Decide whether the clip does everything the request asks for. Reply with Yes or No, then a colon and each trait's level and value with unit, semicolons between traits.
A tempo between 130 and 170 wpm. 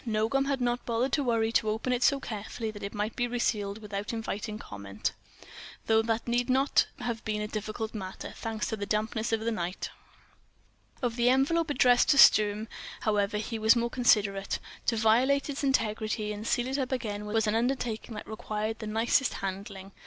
No: average, 190 wpm